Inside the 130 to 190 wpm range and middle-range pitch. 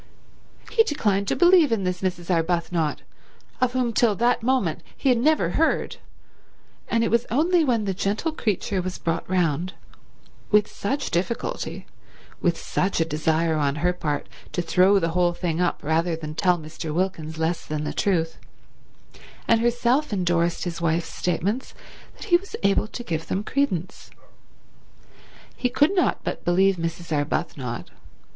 Yes: average, 150 wpm; medium, 180 Hz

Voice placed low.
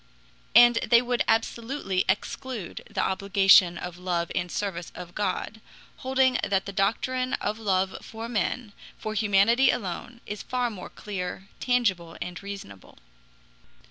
No: high, 200 Hz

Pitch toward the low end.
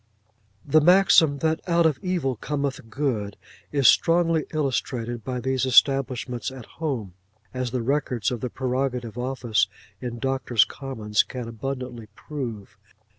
Yes: low, 130 Hz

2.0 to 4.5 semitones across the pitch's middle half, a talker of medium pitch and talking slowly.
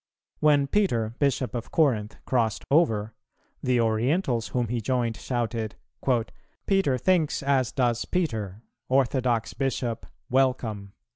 No: average, 3.4 semitones; low, 125 Hz; slow, 115 wpm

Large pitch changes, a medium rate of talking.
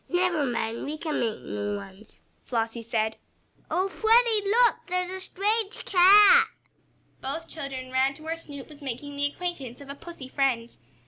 Yes: wide, 6.8 semitones; average, 165 wpm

